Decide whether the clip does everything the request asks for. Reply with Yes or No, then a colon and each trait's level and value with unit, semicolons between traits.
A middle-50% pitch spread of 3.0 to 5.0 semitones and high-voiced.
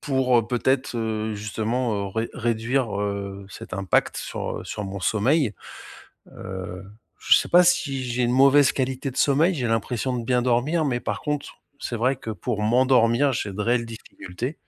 No: average, 3.7 semitones; low, 120 Hz